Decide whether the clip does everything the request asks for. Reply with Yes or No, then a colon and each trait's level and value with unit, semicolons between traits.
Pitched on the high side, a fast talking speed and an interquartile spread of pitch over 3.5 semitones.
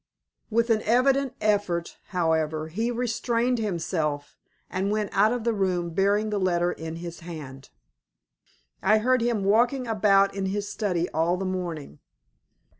No: high, 195 Hz; average, 145 wpm; average, 4.5 semitones